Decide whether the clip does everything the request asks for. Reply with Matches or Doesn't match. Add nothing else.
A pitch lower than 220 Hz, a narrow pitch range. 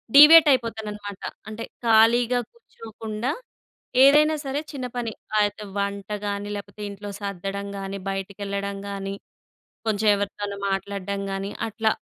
Matches